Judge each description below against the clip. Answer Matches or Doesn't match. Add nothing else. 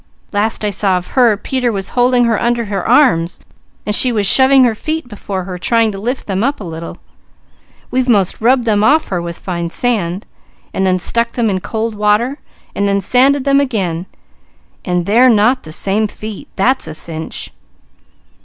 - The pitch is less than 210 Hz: Doesn't match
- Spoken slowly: Doesn't match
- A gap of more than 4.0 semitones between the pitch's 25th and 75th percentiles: Matches